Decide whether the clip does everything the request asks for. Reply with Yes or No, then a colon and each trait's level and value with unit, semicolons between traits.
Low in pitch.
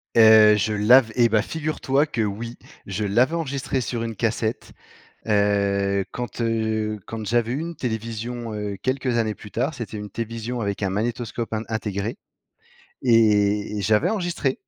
Yes: low, 115 Hz